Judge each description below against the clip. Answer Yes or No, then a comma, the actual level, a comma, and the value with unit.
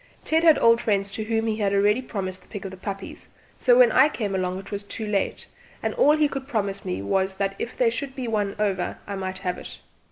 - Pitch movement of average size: Yes, average, 3.4 semitones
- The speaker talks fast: Yes, fast, 250 wpm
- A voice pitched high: Yes, high, 205 Hz